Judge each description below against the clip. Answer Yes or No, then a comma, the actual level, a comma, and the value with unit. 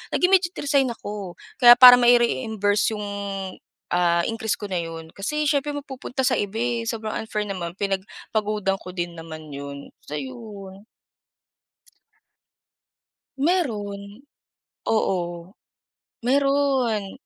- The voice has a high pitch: Yes, high, 210 Hz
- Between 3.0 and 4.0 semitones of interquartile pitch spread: No, average, 5.2 semitones